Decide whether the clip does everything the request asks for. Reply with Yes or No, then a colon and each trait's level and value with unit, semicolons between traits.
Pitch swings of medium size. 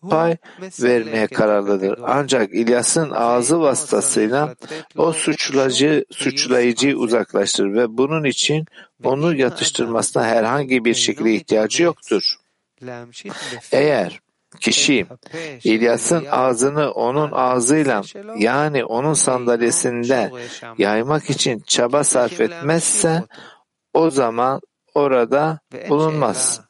Yes: average, 4.5 semitones